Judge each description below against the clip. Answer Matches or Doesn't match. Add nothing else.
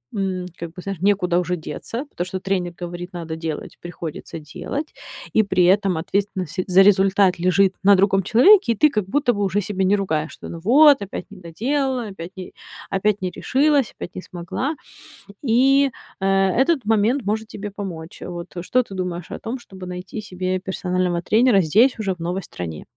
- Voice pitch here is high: Matches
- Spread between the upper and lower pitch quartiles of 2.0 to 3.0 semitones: Doesn't match